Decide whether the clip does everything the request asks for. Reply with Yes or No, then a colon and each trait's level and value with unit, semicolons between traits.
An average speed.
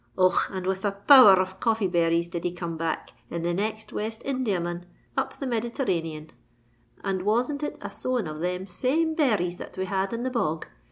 Yes: average, 190 wpm